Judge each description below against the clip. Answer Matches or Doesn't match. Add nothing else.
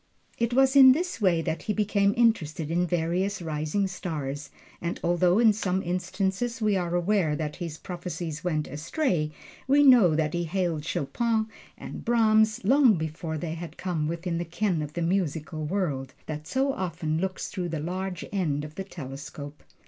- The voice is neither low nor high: Matches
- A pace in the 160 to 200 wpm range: Matches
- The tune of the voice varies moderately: Matches